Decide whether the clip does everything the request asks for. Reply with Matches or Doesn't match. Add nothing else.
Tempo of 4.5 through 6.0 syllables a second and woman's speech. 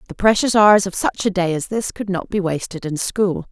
Matches